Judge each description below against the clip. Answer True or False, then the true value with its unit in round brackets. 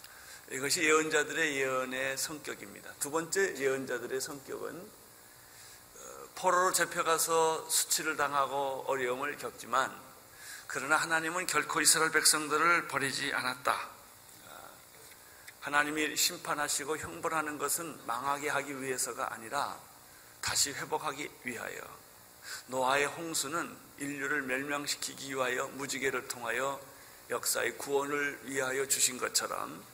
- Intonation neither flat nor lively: True (3.6 semitones)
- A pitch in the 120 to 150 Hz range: True (140 Hz)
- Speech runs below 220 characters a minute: False (290 characters per minute)